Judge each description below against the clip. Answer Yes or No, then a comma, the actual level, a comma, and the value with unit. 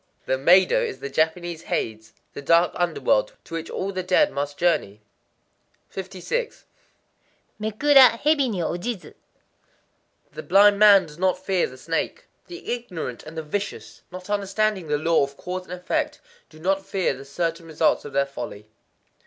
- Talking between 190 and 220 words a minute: No, average, 155 wpm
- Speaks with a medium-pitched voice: Yes, medium, 180 Hz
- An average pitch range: Yes, average, 4.6 semitones